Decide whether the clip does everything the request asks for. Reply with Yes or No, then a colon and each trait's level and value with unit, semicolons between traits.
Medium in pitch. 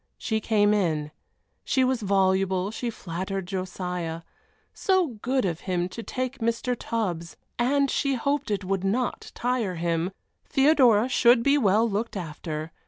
No: high, 205 Hz